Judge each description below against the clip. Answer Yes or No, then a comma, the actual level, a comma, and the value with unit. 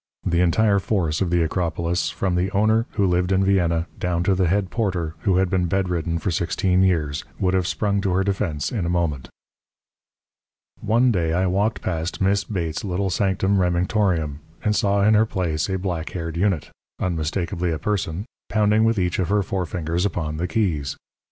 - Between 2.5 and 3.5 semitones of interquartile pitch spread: Yes, average, 2.8 semitones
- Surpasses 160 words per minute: Yes, average, 185 wpm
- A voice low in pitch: Yes, very low, 90 Hz